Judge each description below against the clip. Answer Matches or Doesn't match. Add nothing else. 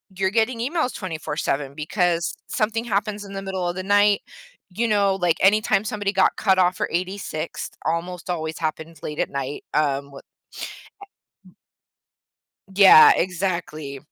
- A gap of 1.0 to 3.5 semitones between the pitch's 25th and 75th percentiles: Doesn't match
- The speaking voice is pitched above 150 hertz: Matches